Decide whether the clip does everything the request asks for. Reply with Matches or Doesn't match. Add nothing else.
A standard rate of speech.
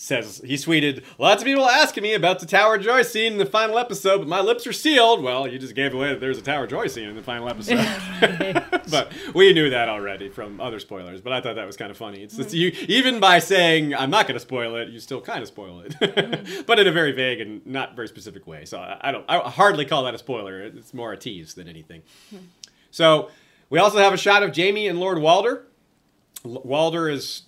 Doesn't match